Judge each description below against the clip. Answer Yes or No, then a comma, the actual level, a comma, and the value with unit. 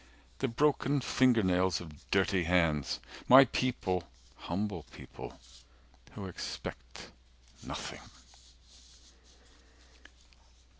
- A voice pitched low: Yes, very low, 95 Hz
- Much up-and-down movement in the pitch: Yes, wide, 6.3 semitones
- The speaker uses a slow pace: Yes, slow, 80 wpm